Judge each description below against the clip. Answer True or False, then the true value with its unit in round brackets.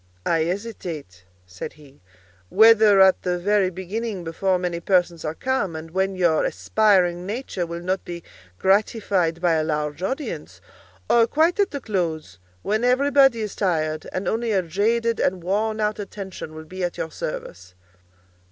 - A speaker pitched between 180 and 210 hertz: True (185 Hz)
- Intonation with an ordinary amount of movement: True (4.6 semitones)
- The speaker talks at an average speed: True (160 wpm)